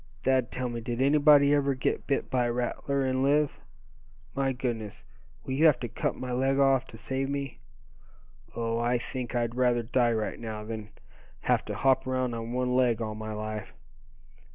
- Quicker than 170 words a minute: Yes, average, 185 wpm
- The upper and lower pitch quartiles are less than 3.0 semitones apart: Yes, narrow, 2.4 semitones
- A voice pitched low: Yes, low, 125 Hz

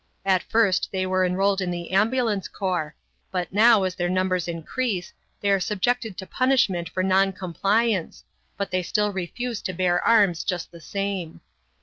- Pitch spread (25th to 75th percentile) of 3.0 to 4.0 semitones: No, narrow, 2.5 semitones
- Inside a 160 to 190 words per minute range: Yes, average, 165 wpm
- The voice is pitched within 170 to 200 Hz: Yes, high, 190 Hz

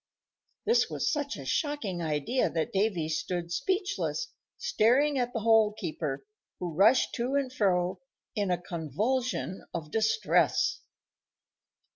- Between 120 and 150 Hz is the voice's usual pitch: No, high, 215 Hz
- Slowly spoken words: Yes, slow, 125 wpm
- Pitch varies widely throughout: Yes, wide, 7.1 semitones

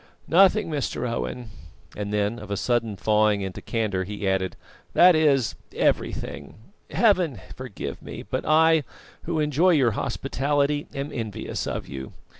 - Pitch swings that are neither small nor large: No, wide, 6.6 semitones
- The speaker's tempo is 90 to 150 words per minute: Yes, slow, 135 wpm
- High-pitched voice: No, low, 125 Hz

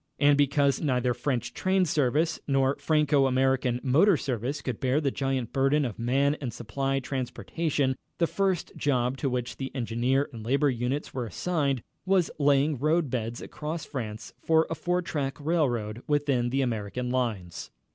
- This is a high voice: No, low, 135 Hz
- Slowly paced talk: No, average, 160 wpm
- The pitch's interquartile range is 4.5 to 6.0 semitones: No, average, 3.2 semitones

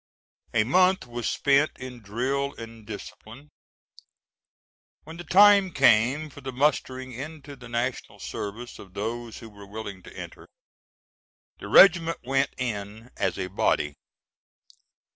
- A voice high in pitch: No, low, 125 Hz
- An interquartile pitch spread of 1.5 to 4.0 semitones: No, average, 4.5 semitones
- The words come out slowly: Yes, slow, 130 wpm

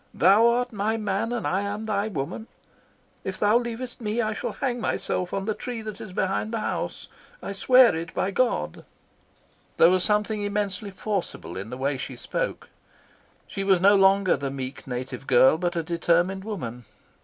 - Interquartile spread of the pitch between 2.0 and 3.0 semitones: No, average, 4.4 semitones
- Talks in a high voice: Yes, high, 200 Hz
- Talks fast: No, average, 185 wpm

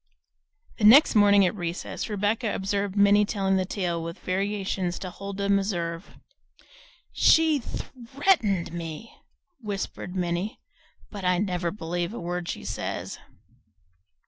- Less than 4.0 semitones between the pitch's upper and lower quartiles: Yes, average, 2.8 semitones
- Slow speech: Yes, slow, 120 wpm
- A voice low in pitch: No, high, 195 Hz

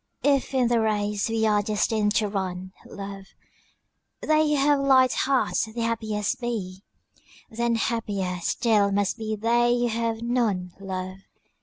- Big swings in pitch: No, average, 3.0 semitones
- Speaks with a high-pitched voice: Yes, high, 220 Hz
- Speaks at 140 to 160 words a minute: Yes, average, 145 wpm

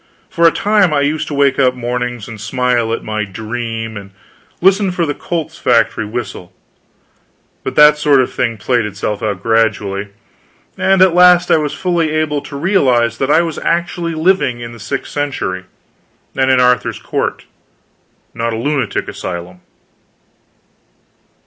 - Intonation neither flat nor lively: No, wide, 5.9 semitones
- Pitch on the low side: Yes, low, 125 Hz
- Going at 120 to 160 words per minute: Yes, average, 155 wpm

